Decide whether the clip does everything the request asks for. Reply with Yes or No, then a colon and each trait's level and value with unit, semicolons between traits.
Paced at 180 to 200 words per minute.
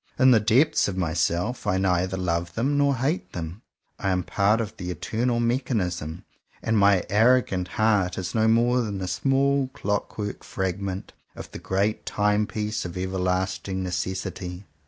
No: average, 160 wpm